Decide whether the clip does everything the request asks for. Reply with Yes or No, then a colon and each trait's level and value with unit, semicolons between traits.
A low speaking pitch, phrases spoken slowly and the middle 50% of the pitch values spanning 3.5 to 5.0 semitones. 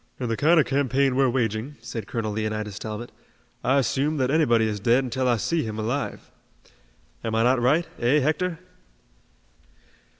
No: low, 125 Hz; average, 165 wpm; average, 3.8 semitones